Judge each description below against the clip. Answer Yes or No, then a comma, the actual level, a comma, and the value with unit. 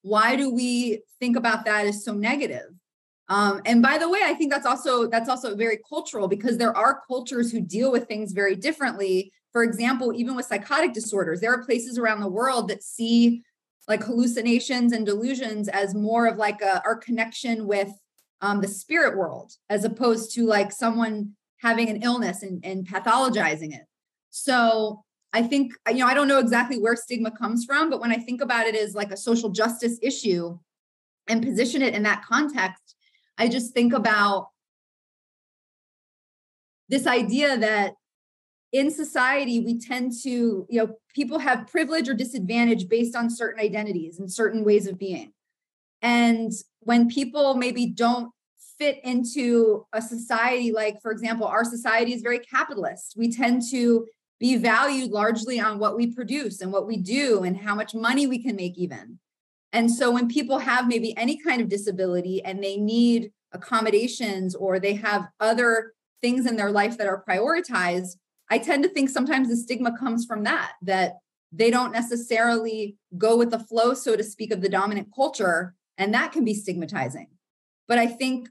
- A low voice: No, high, 230 Hz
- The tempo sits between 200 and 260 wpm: No, average, 175 wpm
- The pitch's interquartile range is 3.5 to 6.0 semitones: No, average, 2.9 semitones